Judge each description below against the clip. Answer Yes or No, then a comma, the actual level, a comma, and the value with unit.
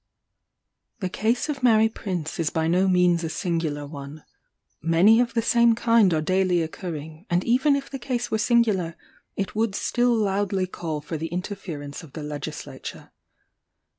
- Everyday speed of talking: Yes, average, 165 wpm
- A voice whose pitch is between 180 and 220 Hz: Yes, medium, 185 Hz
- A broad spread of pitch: Yes, wide, 5.7 semitones